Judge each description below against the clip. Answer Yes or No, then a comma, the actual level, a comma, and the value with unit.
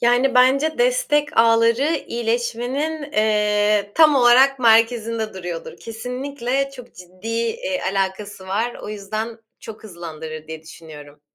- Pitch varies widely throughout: No, average, 4.3 semitones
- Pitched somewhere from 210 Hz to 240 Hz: Yes, high, 230 Hz